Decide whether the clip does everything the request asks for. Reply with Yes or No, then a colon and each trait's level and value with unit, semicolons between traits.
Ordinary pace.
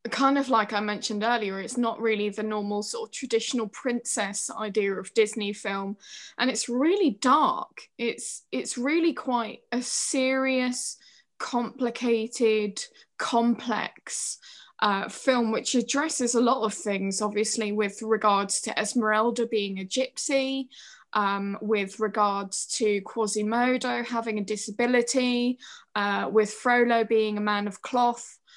No: slow, 130 wpm